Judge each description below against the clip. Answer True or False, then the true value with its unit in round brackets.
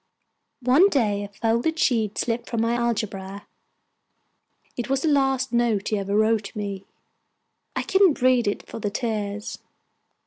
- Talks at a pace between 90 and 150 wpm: True (145 wpm)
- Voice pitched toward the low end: False (230 Hz)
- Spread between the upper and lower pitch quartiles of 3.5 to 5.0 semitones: True (3.8 semitones)